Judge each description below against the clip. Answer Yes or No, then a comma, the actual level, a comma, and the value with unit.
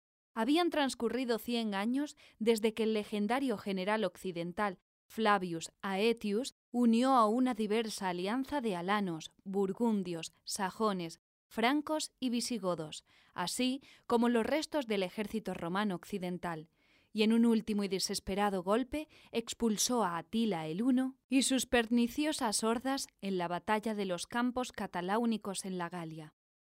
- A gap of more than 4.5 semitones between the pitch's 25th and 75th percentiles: No, average, 4.0 semitones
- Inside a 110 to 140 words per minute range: Yes, average, 130 wpm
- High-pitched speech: Yes, high, 220 Hz